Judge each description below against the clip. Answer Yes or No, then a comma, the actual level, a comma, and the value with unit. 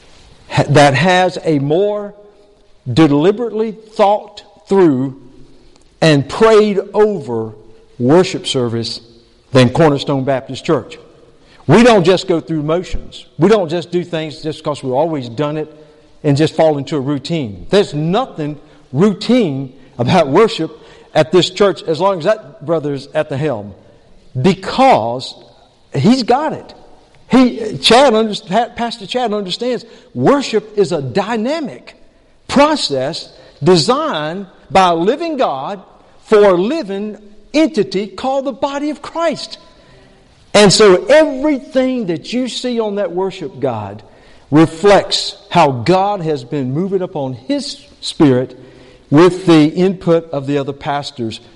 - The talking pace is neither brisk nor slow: No, slow, 125 wpm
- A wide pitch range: Yes, wide, 6.5 semitones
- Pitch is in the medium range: Yes, medium, 175 Hz